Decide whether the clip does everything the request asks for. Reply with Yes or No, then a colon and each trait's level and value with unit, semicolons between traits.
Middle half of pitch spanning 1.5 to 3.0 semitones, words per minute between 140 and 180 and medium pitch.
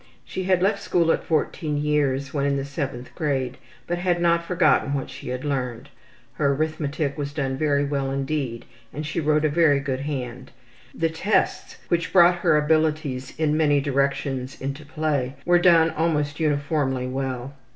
Yes: average, 2.7 semitones; average, 170 wpm; medium, 145 Hz